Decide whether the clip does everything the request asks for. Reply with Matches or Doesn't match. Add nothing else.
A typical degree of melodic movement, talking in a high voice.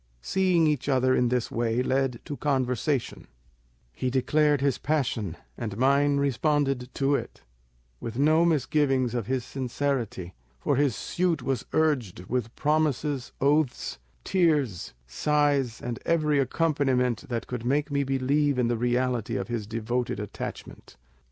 Doesn't match